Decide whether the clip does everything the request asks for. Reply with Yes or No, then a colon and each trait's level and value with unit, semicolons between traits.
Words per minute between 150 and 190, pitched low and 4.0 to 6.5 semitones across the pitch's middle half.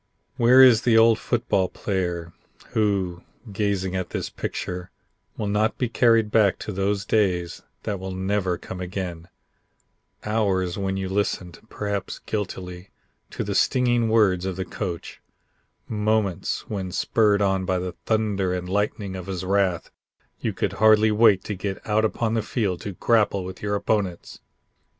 No: average, 155 wpm; low, 100 Hz; average, 2.7 semitones